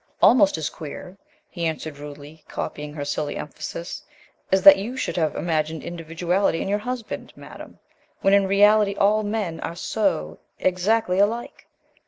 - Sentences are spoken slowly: No, average, 150 wpm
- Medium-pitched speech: Yes, medium, 180 Hz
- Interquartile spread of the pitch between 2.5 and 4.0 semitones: No, average, 4.4 semitones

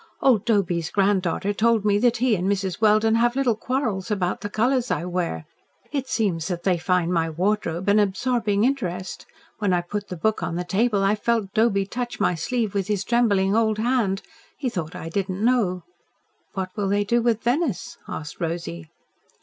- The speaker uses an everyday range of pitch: Yes, average, 4.1 semitones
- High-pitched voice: Yes, high, 205 Hz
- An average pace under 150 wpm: No, average, 190 wpm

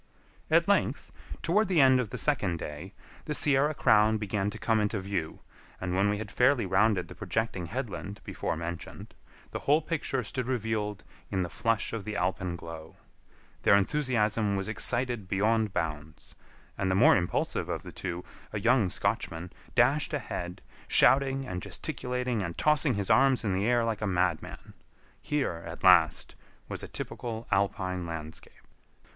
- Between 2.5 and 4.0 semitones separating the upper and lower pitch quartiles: No, average, 5.2 semitones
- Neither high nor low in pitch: No, low, 105 Hz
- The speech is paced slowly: No, average, 160 wpm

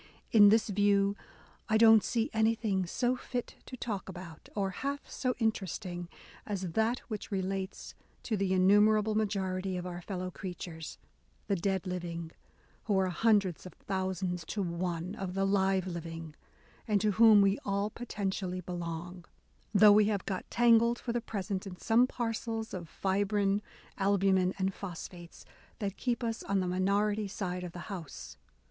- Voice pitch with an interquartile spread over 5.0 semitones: No, average, 2.8 semitones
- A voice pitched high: Yes, high, 195 Hz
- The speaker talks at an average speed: Yes, average, 160 wpm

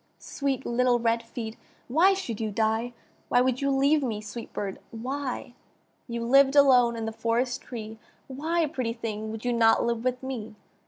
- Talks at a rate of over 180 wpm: No, average, 175 wpm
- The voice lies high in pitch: Yes, high, 240 Hz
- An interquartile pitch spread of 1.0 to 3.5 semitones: Yes, average, 2.9 semitones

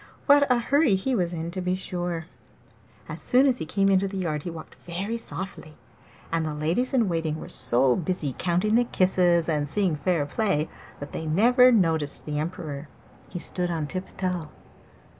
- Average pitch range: Yes, average, 3.9 semitones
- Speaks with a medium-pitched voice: Yes, medium, 175 Hz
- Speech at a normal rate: Yes, average, 180 wpm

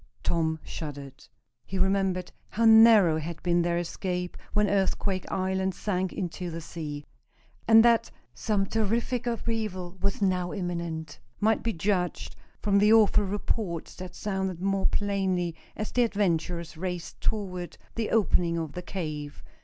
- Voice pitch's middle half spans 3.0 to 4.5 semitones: Yes, average, 3.3 semitones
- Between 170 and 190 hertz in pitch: Yes, medium, 185 Hz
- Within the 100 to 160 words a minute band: Yes, average, 140 wpm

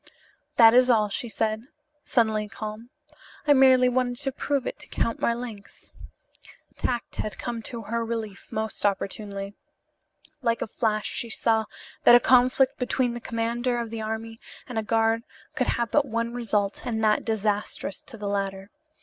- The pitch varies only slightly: Yes, narrow, 2.2 semitones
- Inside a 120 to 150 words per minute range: No, average, 165 wpm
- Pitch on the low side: No, high, 230 Hz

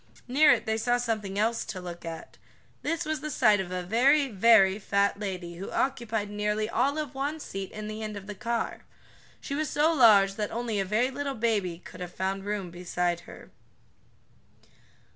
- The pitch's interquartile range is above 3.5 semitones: Yes, average, 4.2 semitones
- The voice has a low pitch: No, high, 215 Hz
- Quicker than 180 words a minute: Yes, average, 190 wpm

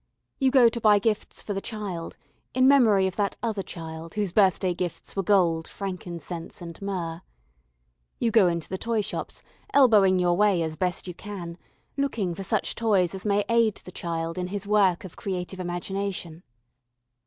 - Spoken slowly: No, average, 170 wpm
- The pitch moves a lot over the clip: No, average, 3.2 semitones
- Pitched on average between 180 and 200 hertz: Yes, high, 190 Hz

